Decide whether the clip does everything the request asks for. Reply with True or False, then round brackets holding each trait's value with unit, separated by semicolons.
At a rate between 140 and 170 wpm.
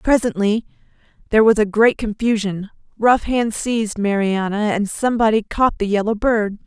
True (145 wpm)